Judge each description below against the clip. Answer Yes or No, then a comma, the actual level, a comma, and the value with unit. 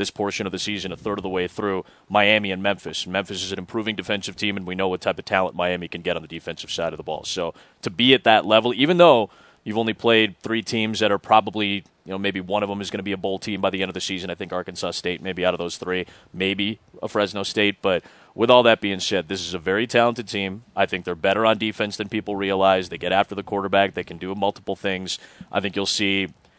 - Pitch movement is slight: Yes, narrow, 2.3 semitones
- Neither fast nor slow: No, fast, 270 wpm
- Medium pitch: No, low, 100 Hz